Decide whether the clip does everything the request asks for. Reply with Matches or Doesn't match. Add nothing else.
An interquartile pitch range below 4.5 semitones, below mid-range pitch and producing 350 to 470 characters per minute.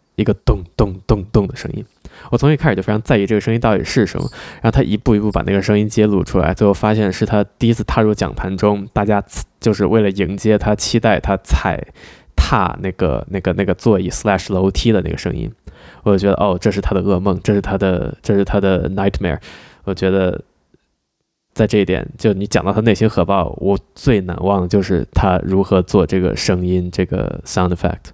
Matches